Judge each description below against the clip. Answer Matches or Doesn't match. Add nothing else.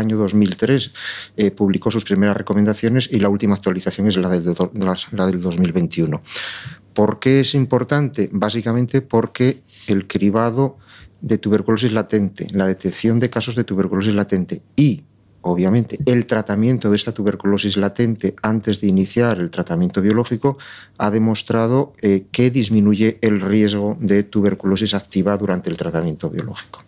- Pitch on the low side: Matches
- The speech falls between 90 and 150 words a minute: Matches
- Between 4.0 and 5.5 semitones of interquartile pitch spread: Doesn't match